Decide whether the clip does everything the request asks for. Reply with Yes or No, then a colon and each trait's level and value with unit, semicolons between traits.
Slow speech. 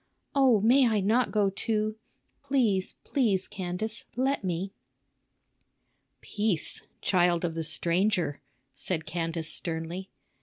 Yes: slow, 110 wpm